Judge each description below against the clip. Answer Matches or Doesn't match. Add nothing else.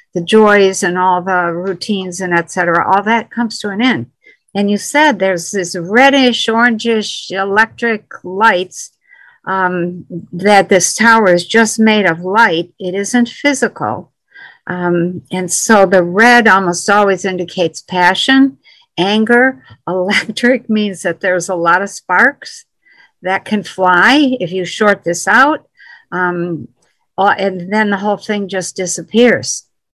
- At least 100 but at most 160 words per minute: Matches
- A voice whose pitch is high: Matches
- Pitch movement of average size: Matches